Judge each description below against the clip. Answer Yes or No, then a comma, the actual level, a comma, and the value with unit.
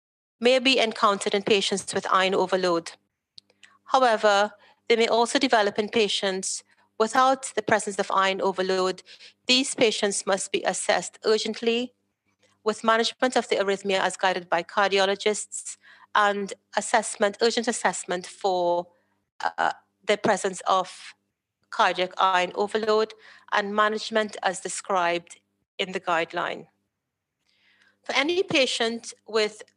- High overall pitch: Yes, high, 205 Hz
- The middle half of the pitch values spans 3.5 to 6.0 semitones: No, average, 3.1 semitones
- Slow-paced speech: Yes, slow, 120 wpm